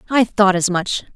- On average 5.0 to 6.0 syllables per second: No, 4.7 syllables/s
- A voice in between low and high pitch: No, high, 200 Hz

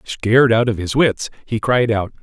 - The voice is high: No, low, 115 Hz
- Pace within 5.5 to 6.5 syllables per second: No, 4.7 syllables/s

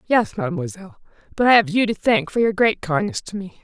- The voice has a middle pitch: No, high, 210 Hz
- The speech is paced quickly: Yes, fast, 230 wpm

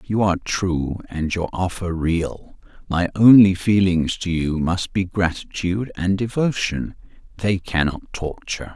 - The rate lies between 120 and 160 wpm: Yes, slow, 135 wpm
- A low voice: Yes, very low, 90 Hz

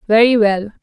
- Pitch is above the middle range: Yes, high, 215 Hz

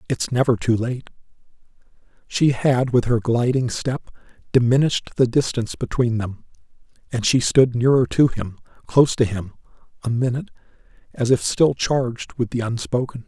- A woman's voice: No, male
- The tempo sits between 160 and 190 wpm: No, average, 150 wpm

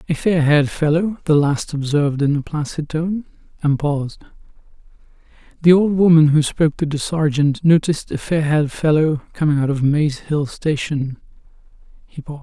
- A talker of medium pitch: Yes, medium, 150 Hz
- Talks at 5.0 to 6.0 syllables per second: Yes, 5.3 syllables/s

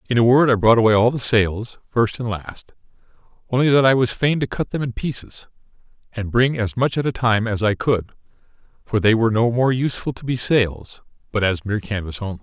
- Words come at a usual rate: No, fast, 220 wpm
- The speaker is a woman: No, male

